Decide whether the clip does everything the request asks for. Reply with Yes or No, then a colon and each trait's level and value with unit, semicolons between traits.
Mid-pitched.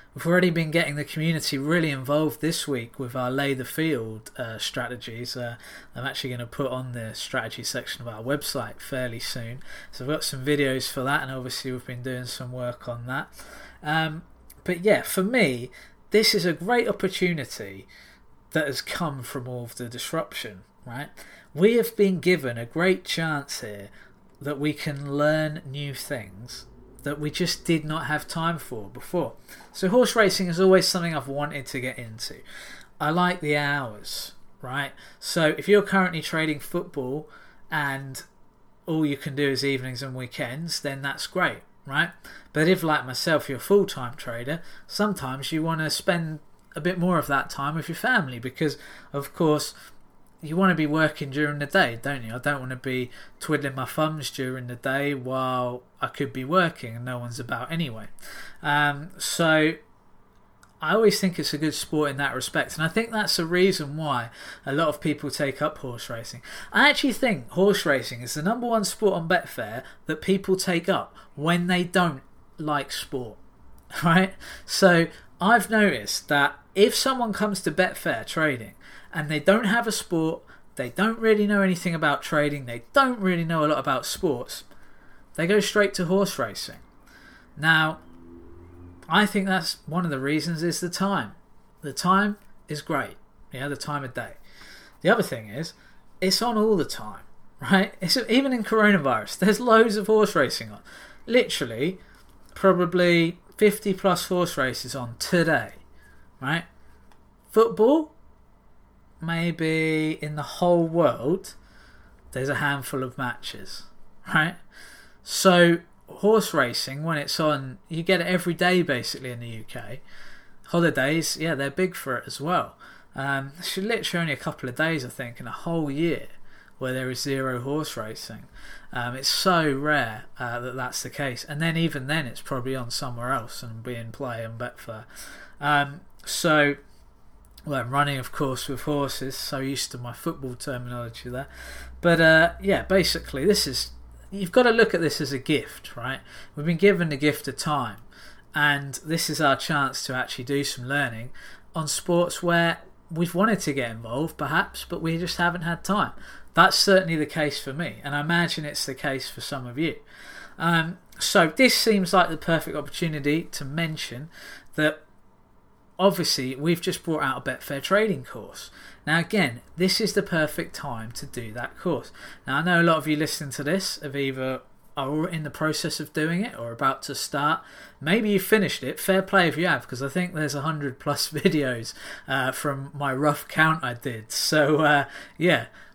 Yes: medium, 150 Hz